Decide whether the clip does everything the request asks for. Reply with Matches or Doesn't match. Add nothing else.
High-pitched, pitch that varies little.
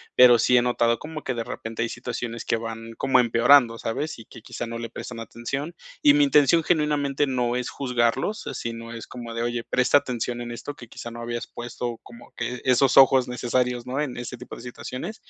Doesn't match